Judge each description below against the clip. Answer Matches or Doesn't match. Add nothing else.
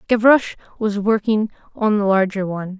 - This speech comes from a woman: Matches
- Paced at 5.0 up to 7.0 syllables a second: Matches